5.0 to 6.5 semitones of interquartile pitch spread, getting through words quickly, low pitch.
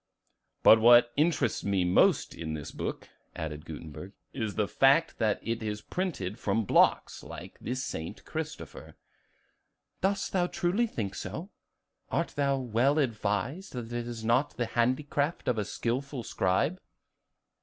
No: wide, 5.5 semitones; average, 145 wpm; low, 120 Hz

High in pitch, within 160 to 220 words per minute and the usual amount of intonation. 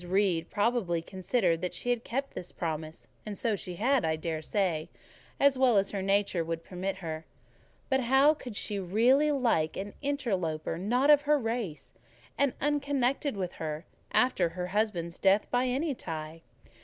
No: high, 200 Hz; average, 165 wpm; wide, 6.9 semitones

